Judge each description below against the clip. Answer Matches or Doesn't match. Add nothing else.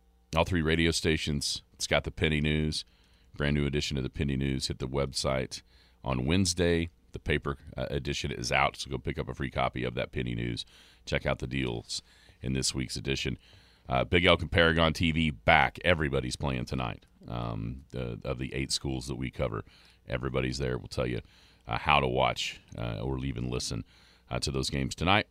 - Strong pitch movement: Doesn't match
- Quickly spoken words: Doesn't match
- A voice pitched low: Matches